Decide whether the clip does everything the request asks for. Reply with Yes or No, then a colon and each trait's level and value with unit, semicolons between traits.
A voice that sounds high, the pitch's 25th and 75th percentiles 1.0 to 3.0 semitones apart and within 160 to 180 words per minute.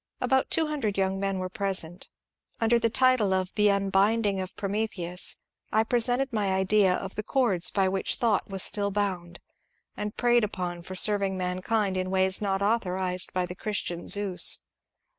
Yes: high, 195 Hz; narrow, 2.6 semitones; average, 165 wpm